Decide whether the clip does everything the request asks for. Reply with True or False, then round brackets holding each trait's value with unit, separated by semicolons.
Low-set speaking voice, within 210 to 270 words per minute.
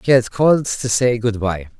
True (120 Hz; 235 wpm)